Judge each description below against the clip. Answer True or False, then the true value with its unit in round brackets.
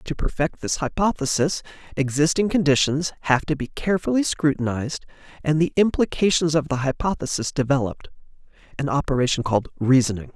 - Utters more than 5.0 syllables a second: True (5.9 syllables/s)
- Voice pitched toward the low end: False (150 Hz)